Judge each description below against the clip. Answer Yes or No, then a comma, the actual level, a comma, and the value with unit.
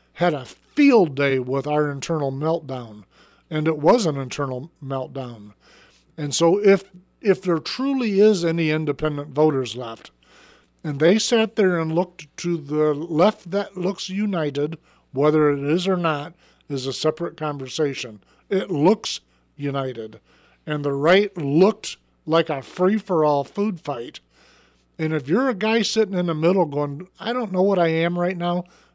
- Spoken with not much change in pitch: No, average, 4.3 semitones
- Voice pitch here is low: No, medium, 160 Hz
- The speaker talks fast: No, average, 160 wpm